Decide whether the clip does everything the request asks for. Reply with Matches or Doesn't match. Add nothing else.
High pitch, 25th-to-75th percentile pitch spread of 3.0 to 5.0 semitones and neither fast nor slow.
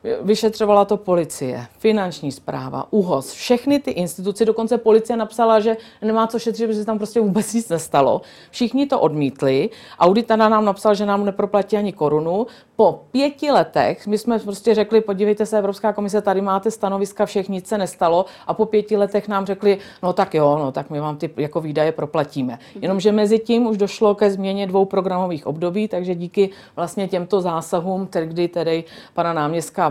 Doesn't match